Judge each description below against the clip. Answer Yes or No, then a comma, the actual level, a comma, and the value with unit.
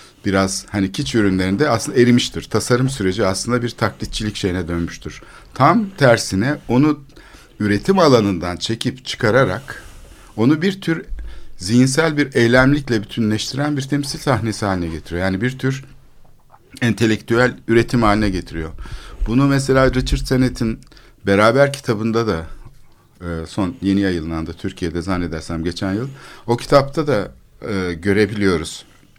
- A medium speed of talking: Yes, average, 115 wpm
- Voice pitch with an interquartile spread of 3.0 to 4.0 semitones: No, wide, 5.5 semitones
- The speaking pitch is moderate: No, low, 115 Hz